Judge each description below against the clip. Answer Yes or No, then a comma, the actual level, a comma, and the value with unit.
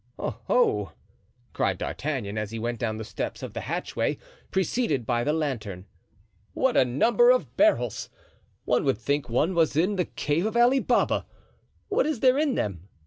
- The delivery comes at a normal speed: Yes, average, 170 wpm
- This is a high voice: No, medium, 150 Hz